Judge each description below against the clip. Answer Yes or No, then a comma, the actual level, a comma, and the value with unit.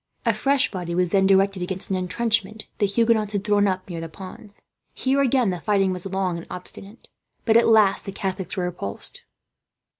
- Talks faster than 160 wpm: Yes, average, 190 wpm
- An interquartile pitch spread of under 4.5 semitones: Yes, average, 2.9 semitones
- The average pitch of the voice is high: Yes, high, 195 Hz